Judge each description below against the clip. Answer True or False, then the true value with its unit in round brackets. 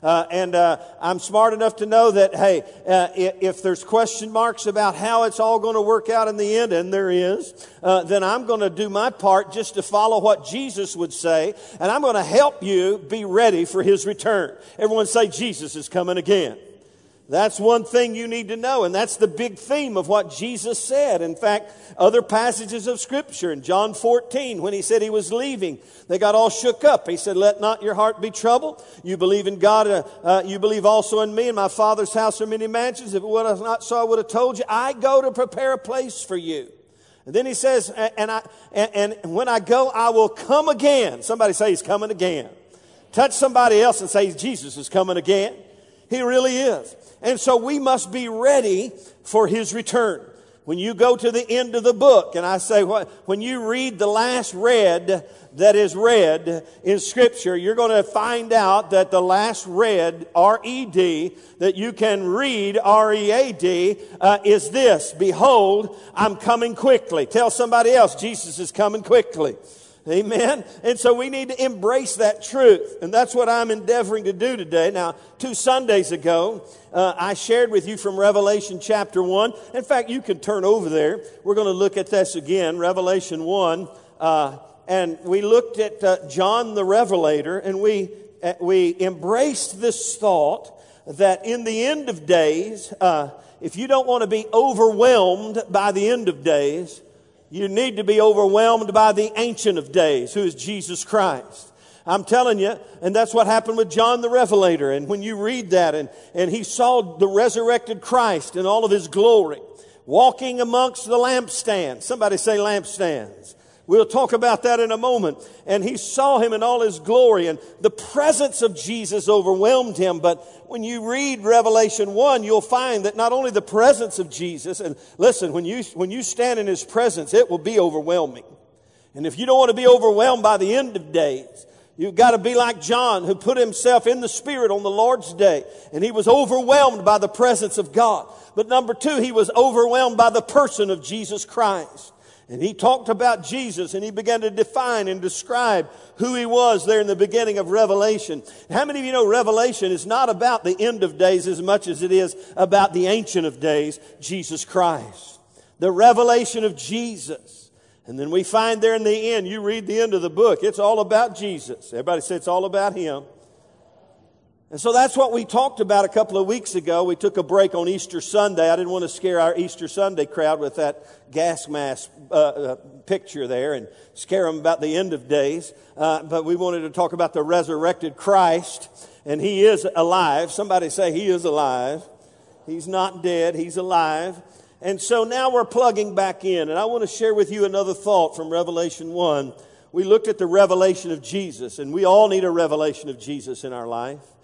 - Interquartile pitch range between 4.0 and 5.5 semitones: True (4.4 semitones)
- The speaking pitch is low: False (210 Hz)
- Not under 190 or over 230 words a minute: True (200 wpm)